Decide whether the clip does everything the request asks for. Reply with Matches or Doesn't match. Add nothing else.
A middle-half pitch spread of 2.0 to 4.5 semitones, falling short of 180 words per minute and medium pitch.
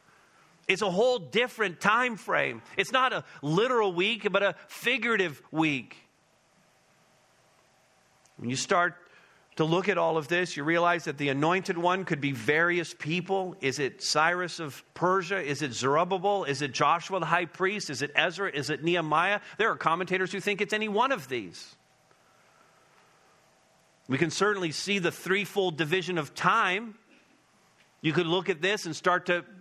Matches